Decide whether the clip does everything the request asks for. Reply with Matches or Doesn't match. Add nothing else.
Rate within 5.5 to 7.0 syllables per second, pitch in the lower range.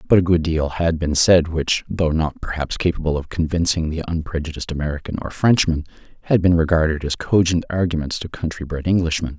Matches